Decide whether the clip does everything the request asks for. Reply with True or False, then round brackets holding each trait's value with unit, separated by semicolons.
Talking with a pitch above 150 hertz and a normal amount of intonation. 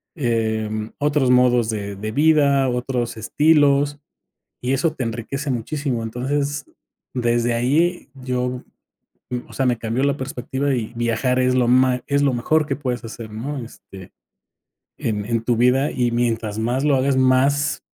False (125 Hz; 3.1 semitones)